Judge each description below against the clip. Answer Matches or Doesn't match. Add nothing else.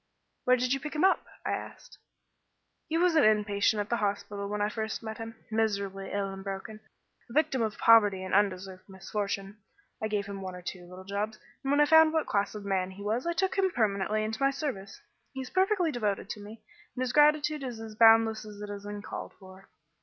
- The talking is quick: Matches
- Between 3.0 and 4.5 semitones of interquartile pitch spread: Matches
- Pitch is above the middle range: Matches